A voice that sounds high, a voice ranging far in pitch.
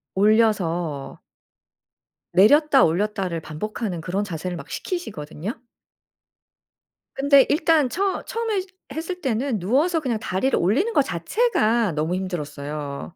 Yes: high, 215 Hz; wide, 8.9 semitones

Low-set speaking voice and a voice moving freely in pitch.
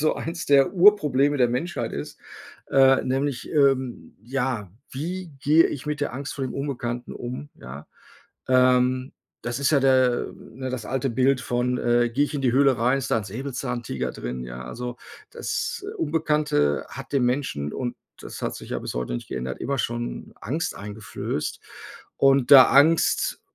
No: low, 130 Hz; average, 2.9 semitones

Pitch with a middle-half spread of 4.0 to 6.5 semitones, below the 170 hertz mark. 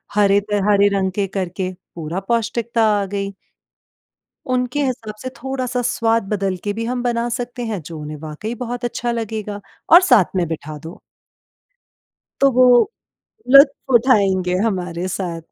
No: average, 4.5 semitones; high, 210 Hz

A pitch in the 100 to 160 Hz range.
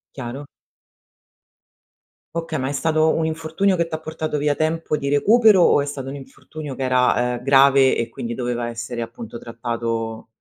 Yes: medium, 140 Hz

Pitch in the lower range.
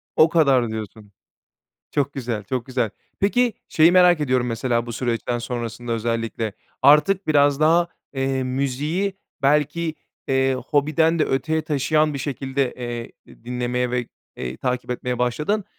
Yes: low, 130 Hz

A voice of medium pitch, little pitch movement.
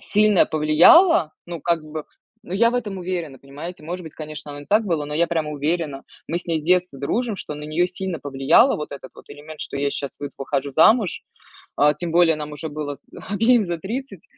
No: medium, 160 Hz; average, 3.7 semitones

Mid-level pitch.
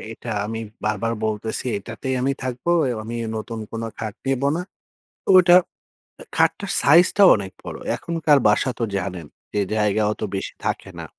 No: low, 115 Hz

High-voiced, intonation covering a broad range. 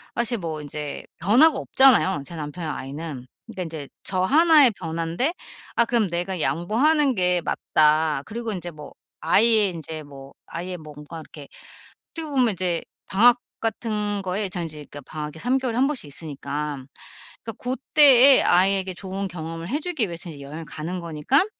No: medium, 180 Hz; wide, 6.9 semitones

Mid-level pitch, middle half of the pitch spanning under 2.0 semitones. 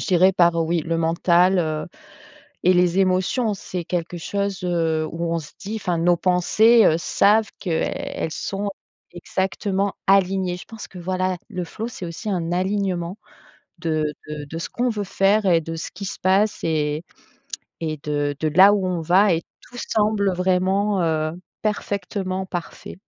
No: medium, 180 Hz; average, 2.9 semitones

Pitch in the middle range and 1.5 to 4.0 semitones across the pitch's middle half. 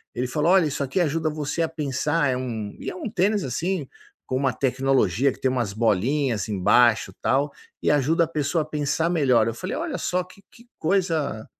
No: medium, 145 Hz; average, 4.7 semitones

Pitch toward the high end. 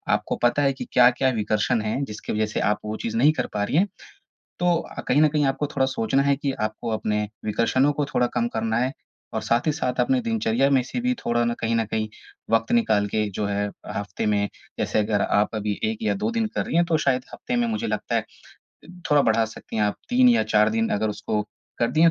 No: low, 125 Hz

